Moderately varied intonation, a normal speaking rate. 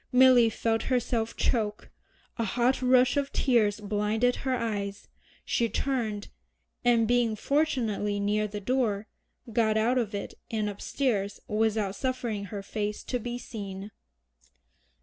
No: average, 3.0 semitones; slow, 130 wpm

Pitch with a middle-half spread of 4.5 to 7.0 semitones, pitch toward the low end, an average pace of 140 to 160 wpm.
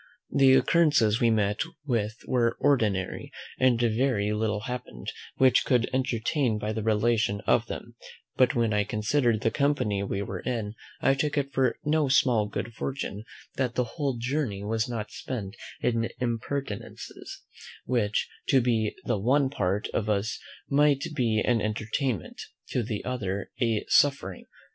No: average, 3.7 semitones; low, 115 Hz; average, 150 wpm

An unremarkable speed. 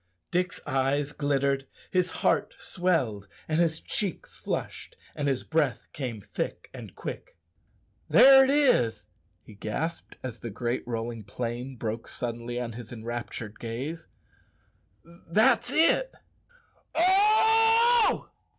No: slow, 120 wpm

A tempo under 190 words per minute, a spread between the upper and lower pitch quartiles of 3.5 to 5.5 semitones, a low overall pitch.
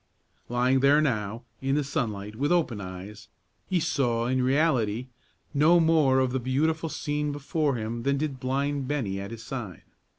Yes: average, 165 wpm; average, 4.1 semitones; low, 130 Hz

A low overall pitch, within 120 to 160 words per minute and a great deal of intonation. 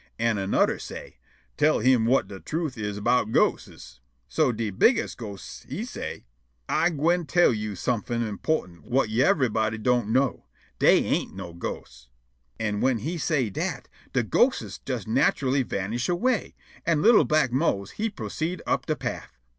Yes: low, 125 Hz; average, 155 wpm; wide, 6.5 semitones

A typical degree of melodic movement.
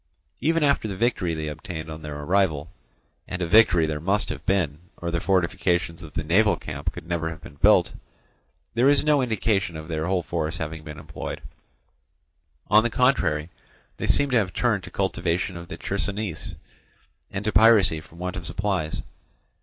Yes: average, 4.6 semitones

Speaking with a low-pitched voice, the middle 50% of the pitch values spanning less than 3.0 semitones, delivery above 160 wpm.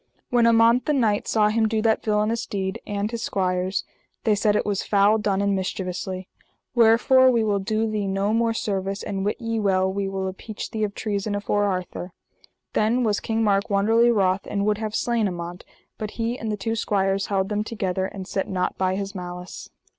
No: high, 205 Hz; narrow, 2.5 semitones; average, 200 wpm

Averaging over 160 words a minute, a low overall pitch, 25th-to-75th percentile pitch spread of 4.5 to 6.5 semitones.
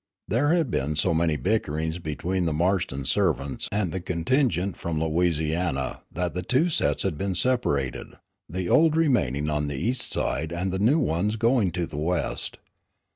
Yes: average, 170 wpm; very low, 90 Hz; wide, 5.4 semitones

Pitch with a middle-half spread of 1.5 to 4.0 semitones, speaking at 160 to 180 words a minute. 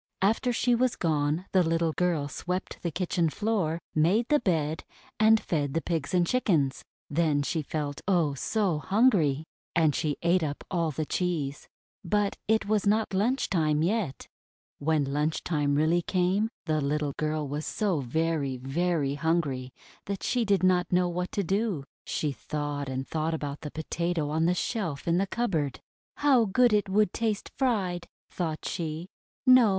No: average, 4.8 semitones; average, 165 wpm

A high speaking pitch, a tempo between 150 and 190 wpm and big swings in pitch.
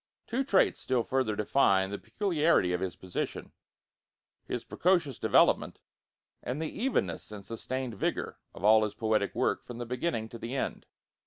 No: low, 120 Hz; average, 160 wpm; wide, 5.9 semitones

